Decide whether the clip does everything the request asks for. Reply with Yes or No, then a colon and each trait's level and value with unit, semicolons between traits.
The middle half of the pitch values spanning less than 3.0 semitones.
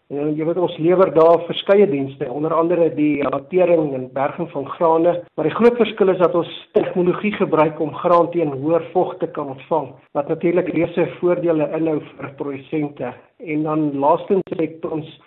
Yes: narrow, 2.6 semitones